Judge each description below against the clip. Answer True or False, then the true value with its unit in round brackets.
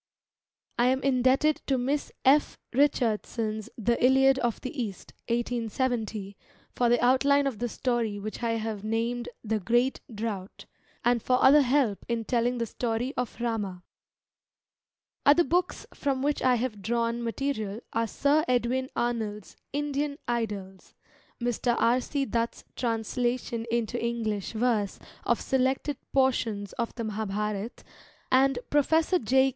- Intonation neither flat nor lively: True (3.0 semitones)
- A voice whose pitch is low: False (240 Hz)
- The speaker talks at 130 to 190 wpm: True (135 wpm)